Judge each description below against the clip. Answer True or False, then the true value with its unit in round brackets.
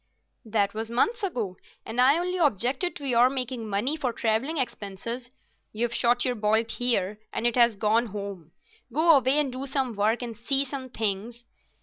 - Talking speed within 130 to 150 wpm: False (180 wpm)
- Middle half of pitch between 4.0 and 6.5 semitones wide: False (3.5 semitones)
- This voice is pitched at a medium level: False (240 Hz)